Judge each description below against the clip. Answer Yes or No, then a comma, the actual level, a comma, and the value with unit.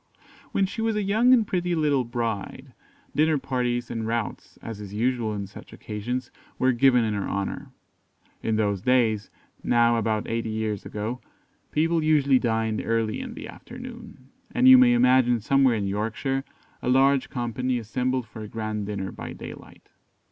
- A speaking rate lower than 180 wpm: Yes, average, 165 wpm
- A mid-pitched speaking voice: No, low, 120 Hz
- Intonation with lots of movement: No, average, 4.1 semitones